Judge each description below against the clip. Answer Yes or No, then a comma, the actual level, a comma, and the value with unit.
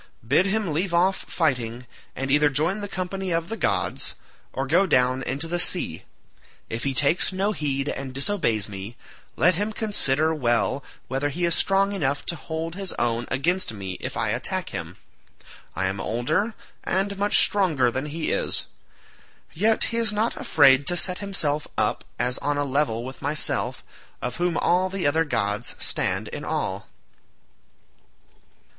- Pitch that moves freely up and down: Yes, wide, 6.1 semitones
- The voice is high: No, medium, 155 Hz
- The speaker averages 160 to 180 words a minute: Yes, average, 165 wpm